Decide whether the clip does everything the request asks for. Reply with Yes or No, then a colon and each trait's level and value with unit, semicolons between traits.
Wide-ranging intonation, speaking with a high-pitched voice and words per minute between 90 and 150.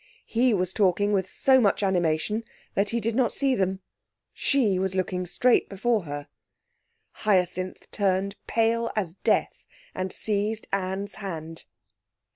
No: average, 3.1 semitones; high, 200 Hz; slow, 135 wpm